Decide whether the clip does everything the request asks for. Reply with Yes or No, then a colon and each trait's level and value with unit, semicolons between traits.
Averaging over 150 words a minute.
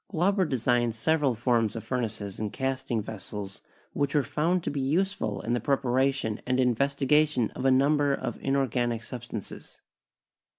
No: average, 145 wpm